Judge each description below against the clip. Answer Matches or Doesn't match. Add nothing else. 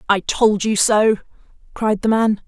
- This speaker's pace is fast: Doesn't match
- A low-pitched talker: Doesn't match